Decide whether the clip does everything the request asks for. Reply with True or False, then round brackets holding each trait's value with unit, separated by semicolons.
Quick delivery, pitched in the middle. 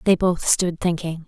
False (190 wpm; 175 Hz)